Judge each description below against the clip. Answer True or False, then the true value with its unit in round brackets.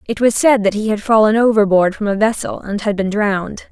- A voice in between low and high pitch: False (210 Hz)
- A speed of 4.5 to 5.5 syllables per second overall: False (5.7 syllables/s)